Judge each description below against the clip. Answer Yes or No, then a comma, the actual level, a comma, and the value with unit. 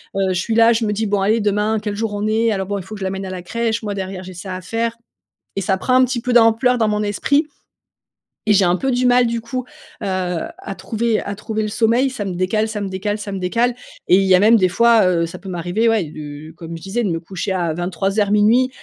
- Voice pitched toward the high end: Yes, high, 205 Hz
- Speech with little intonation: No, average, 3.3 semitones